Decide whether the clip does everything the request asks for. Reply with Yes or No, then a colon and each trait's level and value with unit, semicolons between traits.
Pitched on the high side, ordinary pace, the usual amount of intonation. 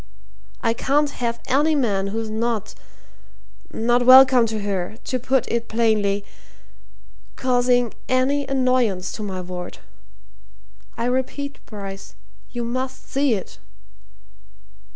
No: high, 235 Hz; slow, 110 wpm; average, 3.5 semitones